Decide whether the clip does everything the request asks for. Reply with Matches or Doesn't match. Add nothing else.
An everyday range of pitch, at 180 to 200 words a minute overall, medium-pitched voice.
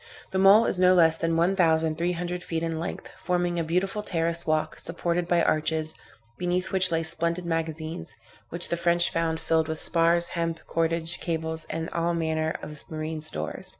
Doesn't match